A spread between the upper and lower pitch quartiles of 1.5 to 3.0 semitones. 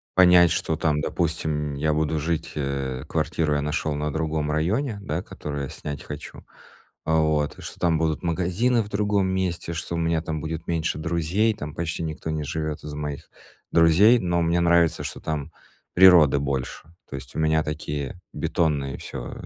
Yes: narrow, 2.4 semitones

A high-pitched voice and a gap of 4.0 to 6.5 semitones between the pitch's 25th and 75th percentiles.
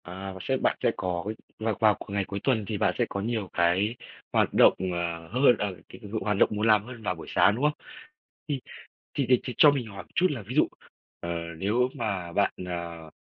No: low, 105 Hz; average, 4.6 semitones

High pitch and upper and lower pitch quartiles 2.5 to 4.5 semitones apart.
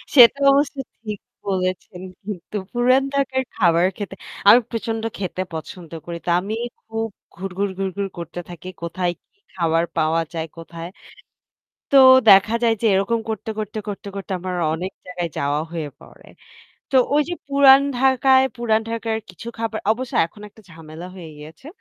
No: high, 195 Hz; average, 5.0 semitones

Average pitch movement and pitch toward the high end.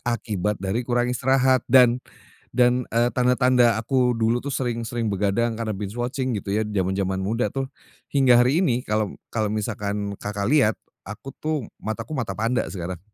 No: average, 3.2 semitones; low, 115 Hz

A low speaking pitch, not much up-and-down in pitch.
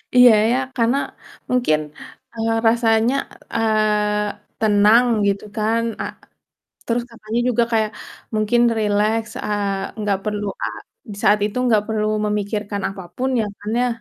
No: high, 215 Hz; narrow, 1.7 semitones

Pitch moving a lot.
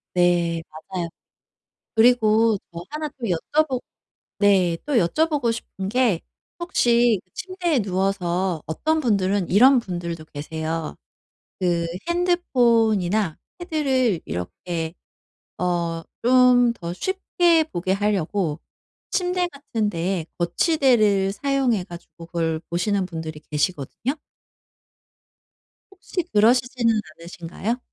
Yes: wide, 6.7 semitones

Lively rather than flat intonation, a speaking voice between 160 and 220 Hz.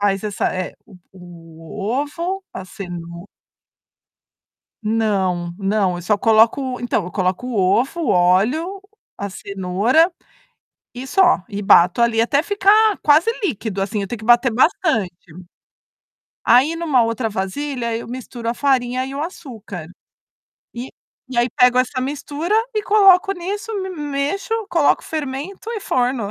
No: wide, 6.9 semitones; high, 245 Hz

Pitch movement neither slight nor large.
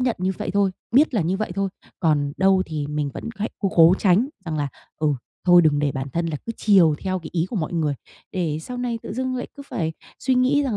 No: wide, 5.9 semitones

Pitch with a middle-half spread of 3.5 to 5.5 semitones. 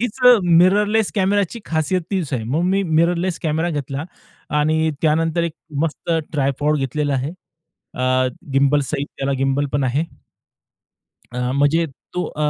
Yes: average, 3.9 semitones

